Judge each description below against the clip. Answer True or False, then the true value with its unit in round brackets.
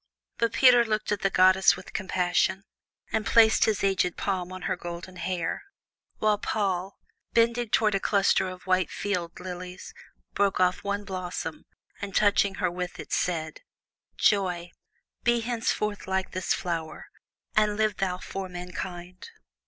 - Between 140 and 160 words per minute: True (145 wpm)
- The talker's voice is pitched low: False (190 Hz)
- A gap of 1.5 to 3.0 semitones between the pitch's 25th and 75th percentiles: True (2.4 semitones)